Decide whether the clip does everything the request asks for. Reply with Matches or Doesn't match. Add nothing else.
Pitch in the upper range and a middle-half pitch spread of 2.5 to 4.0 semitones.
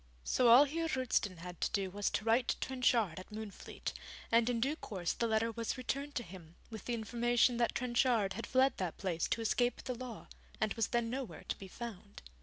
Matches